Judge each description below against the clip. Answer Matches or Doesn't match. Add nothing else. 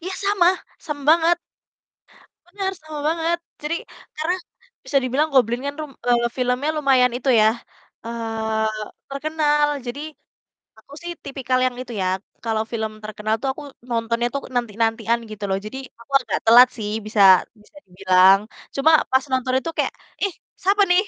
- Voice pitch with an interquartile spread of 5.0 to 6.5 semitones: Matches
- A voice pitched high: Matches